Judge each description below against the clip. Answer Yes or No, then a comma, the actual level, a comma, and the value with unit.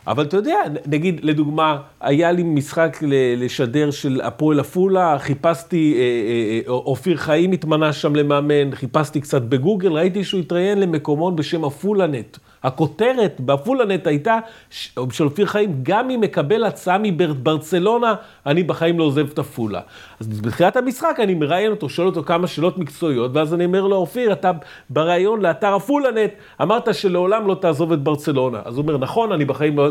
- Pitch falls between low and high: Yes, medium, 160 Hz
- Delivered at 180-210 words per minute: No, average, 155 wpm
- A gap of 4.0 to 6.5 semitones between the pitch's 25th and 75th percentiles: Yes, average, 4.7 semitones